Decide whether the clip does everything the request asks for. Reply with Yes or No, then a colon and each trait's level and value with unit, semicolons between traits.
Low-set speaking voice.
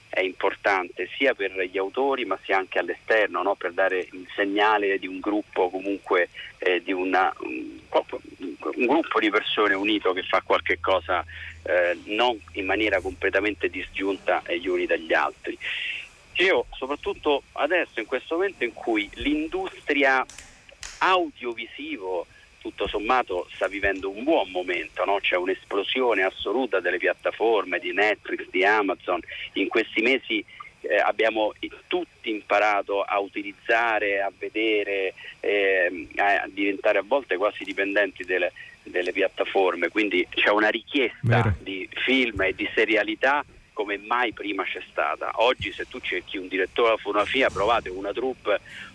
No: very high, 310 Hz